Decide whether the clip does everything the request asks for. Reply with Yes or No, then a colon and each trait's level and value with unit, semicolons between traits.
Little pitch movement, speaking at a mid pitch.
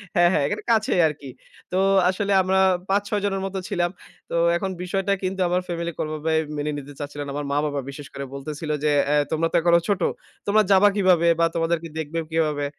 No: average, 4.2 semitones; medium, 170 Hz